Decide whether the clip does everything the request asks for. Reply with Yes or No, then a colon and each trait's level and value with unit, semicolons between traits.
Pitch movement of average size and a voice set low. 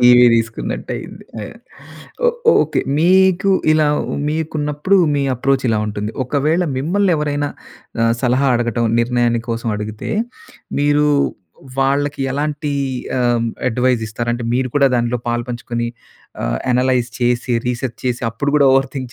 Yes: average, 3.6 semitones; low, 130 Hz